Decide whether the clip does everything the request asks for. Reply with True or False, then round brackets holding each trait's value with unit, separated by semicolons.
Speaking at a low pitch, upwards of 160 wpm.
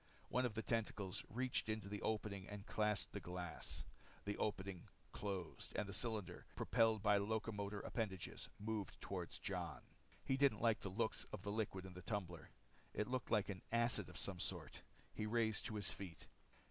True (105 Hz; 175 wpm)